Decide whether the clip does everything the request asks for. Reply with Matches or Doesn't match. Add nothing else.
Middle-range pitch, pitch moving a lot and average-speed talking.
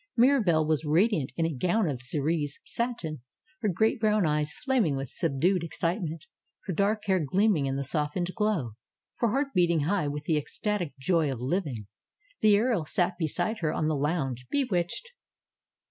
Matches